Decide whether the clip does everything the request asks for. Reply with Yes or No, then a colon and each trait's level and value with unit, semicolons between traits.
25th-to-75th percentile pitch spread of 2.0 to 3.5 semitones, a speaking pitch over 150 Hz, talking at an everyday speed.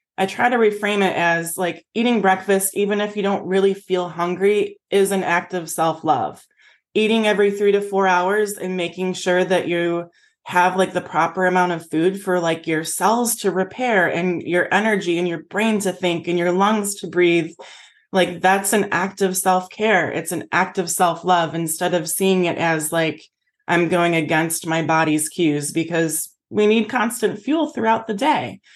Yes: average, 2.9 semitones; medium, 185 Hz; average, 190 wpm